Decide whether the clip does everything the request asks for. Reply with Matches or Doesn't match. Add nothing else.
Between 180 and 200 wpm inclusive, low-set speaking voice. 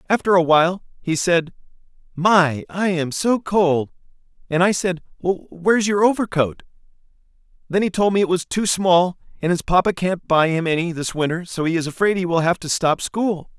Doesn't match